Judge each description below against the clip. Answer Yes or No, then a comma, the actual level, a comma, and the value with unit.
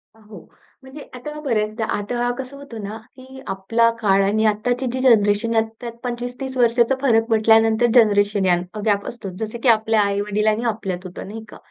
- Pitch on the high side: Yes, high, 225 Hz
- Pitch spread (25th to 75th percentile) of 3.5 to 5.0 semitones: No, average, 2.8 semitones